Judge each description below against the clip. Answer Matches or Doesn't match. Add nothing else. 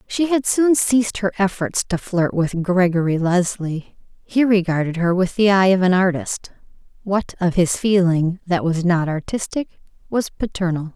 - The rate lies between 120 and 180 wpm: Matches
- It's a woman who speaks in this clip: Matches